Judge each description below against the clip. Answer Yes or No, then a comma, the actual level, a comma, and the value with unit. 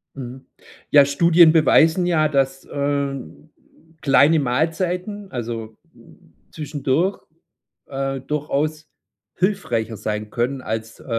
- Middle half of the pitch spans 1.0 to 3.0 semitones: No, average, 3.9 semitones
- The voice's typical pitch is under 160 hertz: Yes, medium, 140 Hz